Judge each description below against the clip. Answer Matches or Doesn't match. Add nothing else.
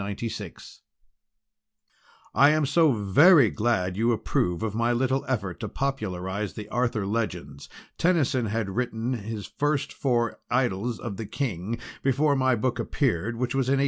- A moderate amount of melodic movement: Matches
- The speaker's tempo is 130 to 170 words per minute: Matches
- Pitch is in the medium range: Doesn't match